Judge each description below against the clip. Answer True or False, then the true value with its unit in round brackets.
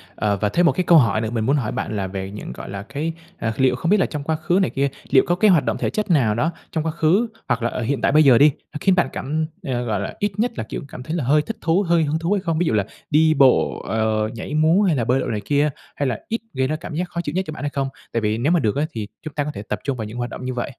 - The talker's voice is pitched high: False (145 Hz)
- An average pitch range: False (6.0 semitones)